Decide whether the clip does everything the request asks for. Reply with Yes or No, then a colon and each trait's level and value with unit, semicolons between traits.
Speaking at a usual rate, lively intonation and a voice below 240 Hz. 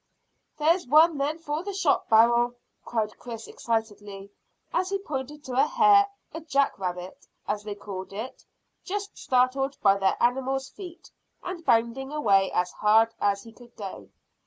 No: average, 160 wpm; wide, 6.6 semitones; very high, 250 Hz